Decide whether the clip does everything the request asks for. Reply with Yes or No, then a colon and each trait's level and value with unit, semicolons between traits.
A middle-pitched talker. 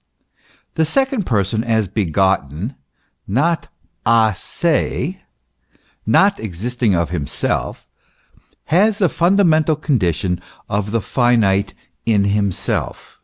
No: low, 110 Hz